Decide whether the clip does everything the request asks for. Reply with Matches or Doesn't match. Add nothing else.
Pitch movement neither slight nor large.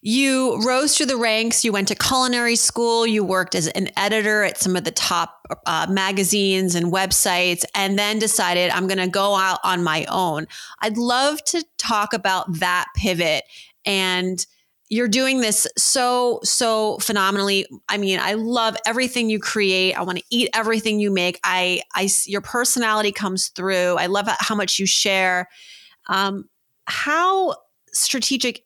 Matches